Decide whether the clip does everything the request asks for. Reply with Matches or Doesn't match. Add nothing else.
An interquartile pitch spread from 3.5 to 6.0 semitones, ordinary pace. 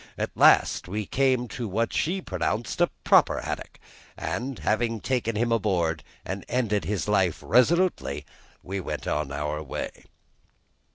Matches